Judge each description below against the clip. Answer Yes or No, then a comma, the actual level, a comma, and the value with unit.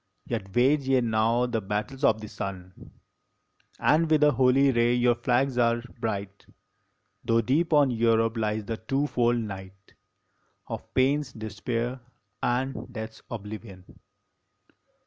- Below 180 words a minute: Yes, average, 140 wpm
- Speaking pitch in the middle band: No, low, 120 Hz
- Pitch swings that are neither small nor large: Yes, average, 3.1 semitones